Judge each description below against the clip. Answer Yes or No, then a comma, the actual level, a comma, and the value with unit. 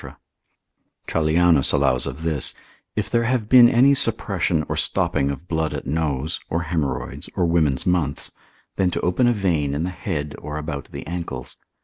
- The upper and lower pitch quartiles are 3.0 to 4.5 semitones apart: Yes, average, 4.2 semitones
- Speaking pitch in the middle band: No, very low, 80 Hz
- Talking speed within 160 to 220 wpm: Yes, average, 165 wpm